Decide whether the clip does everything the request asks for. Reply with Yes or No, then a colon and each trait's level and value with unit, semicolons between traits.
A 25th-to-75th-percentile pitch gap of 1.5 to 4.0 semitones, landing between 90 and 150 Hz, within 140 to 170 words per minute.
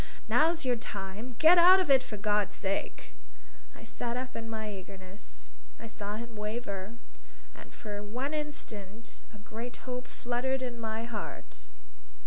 No: average, 3.4 semitones; high, 225 Hz; average, 150 wpm